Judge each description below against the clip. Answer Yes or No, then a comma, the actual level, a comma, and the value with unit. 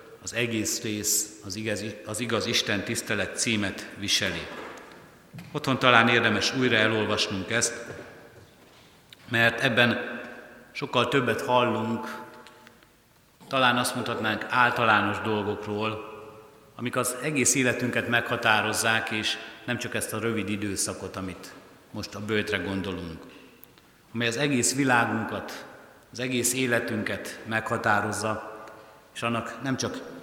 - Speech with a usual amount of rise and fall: No, narrow, 2.3 semitones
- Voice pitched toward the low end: Yes, low, 115 Hz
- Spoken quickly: No, average, 110 wpm